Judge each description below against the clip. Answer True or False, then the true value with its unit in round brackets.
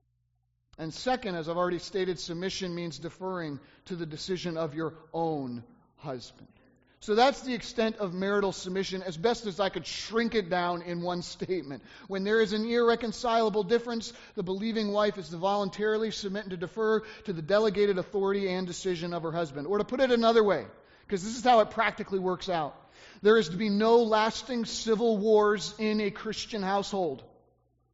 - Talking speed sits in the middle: True (185 wpm)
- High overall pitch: True (195 Hz)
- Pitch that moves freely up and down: False (4.0 semitones)